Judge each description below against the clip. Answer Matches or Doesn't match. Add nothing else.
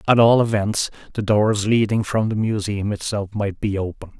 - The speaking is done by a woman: Doesn't match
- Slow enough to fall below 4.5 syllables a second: Doesn't match